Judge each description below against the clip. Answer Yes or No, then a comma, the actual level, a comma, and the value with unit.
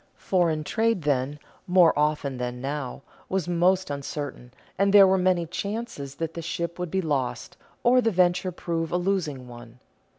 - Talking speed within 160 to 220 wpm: Yes, average, 165 wpm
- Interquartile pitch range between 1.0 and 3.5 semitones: No, average, 4.7 semitones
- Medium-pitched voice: Yes, medium, 170 Hz